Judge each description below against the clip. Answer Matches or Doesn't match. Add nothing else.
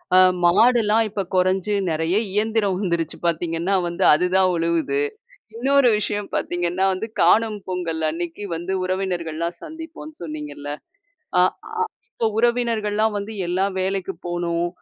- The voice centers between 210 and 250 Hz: Doesn't match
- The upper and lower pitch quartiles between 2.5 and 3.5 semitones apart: Doesn't match